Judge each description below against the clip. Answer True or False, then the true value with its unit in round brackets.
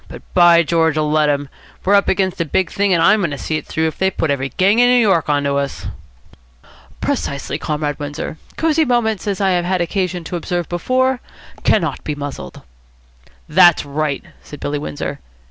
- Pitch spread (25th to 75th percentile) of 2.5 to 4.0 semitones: False (4.7 semitones)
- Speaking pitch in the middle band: True (170 Hz)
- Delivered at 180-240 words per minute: True (195 wpm)